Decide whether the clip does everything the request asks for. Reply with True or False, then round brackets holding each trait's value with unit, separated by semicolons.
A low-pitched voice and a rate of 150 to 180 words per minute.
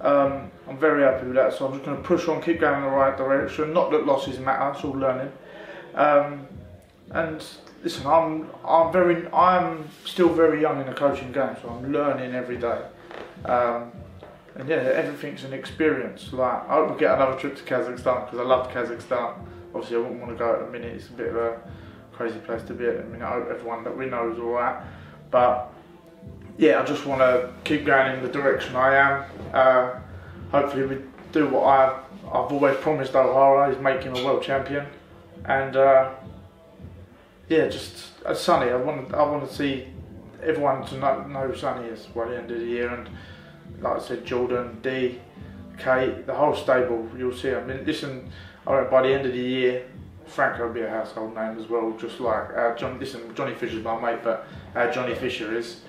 False (130 Hz; 200 wpm)